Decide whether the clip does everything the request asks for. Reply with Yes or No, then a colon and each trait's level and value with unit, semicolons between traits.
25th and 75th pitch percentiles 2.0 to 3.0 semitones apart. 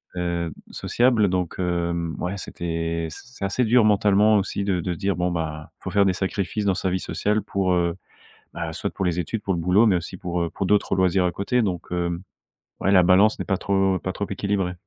Yes: narrow, 2.4 semitones